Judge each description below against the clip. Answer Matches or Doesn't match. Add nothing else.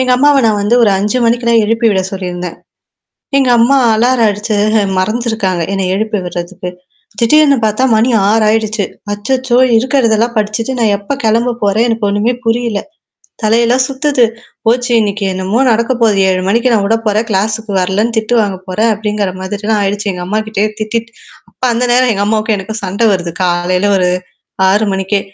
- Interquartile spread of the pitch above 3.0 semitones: Doesn't match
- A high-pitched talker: Matches